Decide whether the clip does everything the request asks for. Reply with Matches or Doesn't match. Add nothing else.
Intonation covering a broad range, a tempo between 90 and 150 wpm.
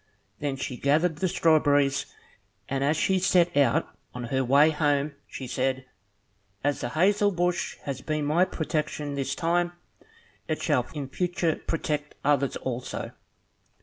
Doesn't match